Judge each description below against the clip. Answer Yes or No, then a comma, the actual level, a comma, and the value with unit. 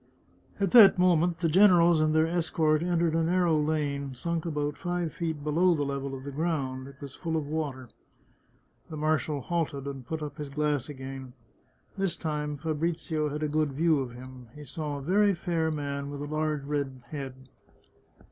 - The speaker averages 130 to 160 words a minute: No, average, 185 wpm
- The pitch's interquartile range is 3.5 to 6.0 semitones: No, average, 2.8 semitones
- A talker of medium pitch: Yes, medium, 150 Hz